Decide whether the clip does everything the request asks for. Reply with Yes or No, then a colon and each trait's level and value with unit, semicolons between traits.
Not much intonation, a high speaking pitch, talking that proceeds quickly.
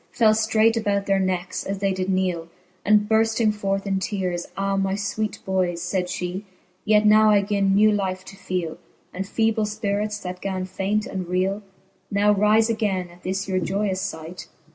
No: narrow, 2.2 semitones; high, 195 Hz; average, 180 wpm